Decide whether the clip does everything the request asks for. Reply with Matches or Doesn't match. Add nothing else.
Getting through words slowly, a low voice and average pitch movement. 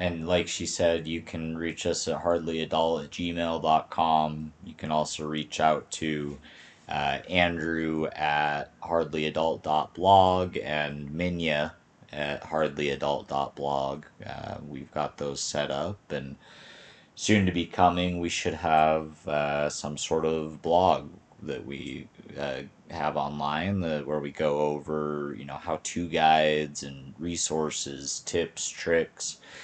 Doesn't match